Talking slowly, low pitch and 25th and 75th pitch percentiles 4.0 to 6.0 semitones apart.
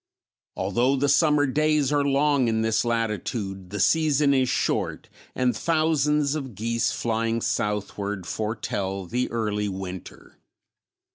Yes: slow, 125 wpm; low, 115 Hz; wide, 5.5 semitones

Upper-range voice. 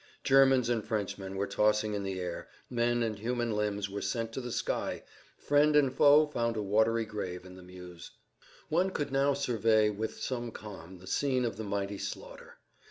No: low, 110 Hz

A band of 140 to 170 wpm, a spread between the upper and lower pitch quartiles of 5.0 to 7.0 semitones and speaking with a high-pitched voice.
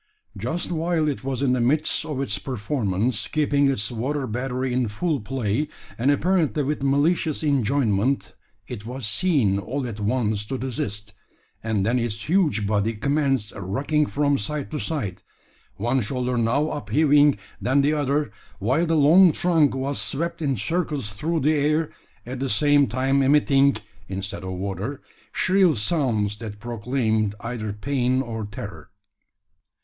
No: average, 150 wpm; average, 5.3 semitones; low, 130 Hz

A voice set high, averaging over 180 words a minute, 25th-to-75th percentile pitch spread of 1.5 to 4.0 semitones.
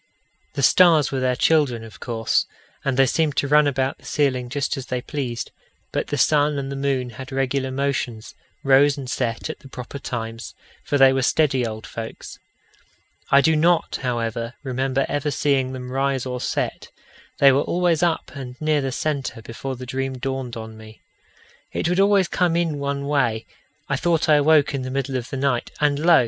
No: low, 135 Hz; average, 195 wpm; narrow, 2.6 semitones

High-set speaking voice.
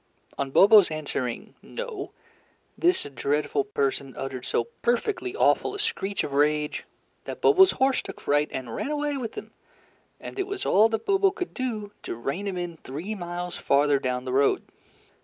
No: medium, 180 Hz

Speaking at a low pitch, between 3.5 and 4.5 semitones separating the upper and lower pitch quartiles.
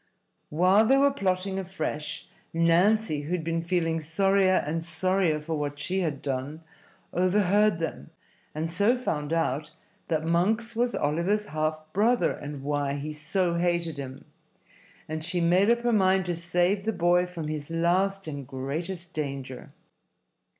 No: medium, 170 Hz; average, 3.8 semitones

